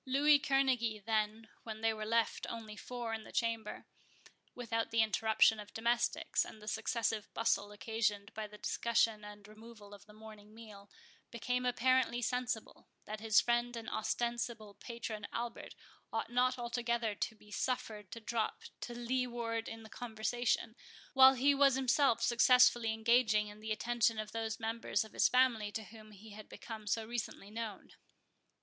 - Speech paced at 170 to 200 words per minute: No, average, 160 wpm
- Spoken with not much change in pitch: Yes, narrow, 1.9 semitones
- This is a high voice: Yes, high, 225 Hz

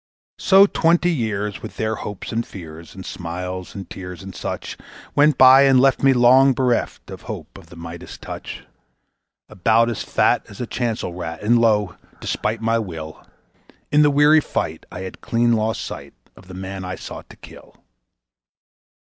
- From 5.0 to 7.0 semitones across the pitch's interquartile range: Yes, wide, 5.6 semitones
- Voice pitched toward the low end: Yes, low, 110 Hz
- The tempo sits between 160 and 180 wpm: Yes, average, 175 wpm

